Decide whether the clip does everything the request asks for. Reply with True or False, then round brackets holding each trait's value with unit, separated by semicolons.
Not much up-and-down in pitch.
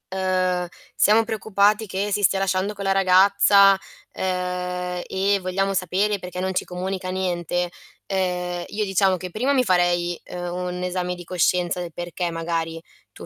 True (1.6 semitones)